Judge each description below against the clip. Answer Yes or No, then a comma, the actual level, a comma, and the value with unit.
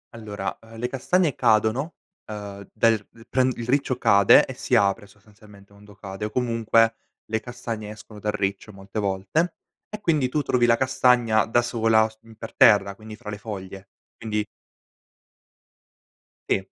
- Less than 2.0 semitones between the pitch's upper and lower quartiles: No, average, 2.8 semitones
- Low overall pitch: Yes, low, 110 Hz